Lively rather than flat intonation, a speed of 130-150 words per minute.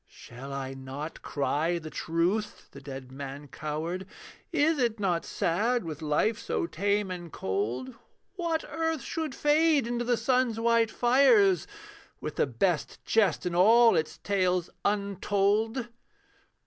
Yes: wide, 7.6 semitones; slow, 135 wpm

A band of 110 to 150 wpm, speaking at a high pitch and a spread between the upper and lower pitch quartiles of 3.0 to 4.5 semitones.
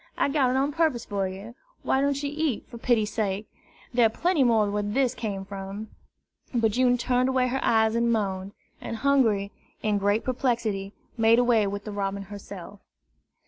No: average, 185 wpm; high, 225 Hz; average, 3.9 semitones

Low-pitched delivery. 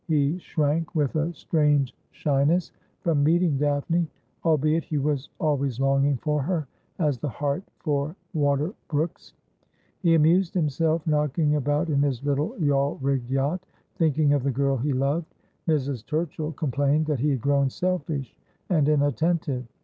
No: medium, 150 Hz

